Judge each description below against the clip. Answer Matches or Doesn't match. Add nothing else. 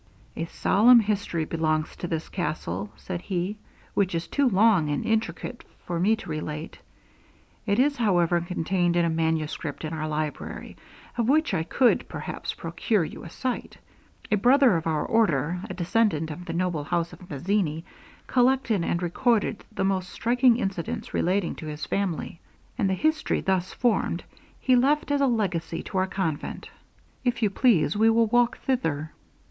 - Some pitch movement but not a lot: Doesn't match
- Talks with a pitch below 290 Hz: Matches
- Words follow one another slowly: Doesn't match